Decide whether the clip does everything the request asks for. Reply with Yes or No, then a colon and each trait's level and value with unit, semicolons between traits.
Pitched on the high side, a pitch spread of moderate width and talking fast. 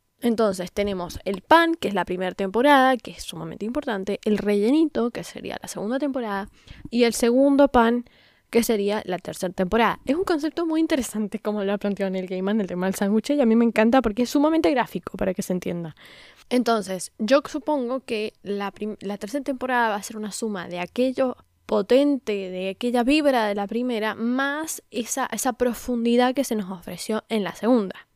Yes: high, 225 Hz; average, 4.3 semitones; fast, 195 wpm